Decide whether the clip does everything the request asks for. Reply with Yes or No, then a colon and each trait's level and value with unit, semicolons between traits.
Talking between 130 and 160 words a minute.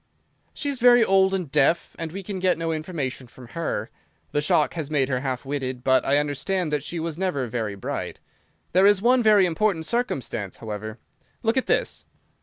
No: average, 195 wpm